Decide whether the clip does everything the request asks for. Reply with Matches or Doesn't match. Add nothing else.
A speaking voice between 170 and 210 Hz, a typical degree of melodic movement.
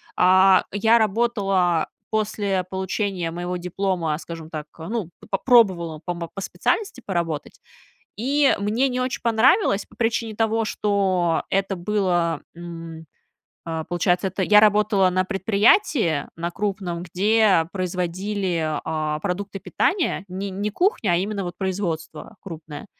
Matches